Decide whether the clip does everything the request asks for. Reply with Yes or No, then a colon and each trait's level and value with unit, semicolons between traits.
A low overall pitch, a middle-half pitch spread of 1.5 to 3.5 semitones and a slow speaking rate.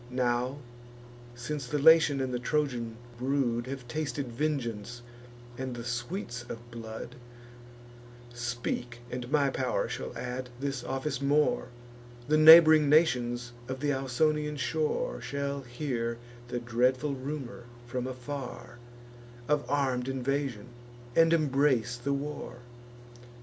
Yes: low, 130 Hz; average, 3.1 semitones; slow, 120 wpm